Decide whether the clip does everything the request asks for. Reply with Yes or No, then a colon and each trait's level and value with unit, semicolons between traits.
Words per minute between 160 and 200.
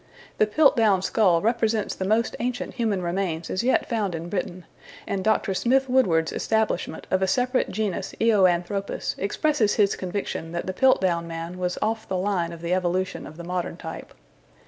Yes: average, 170 wpm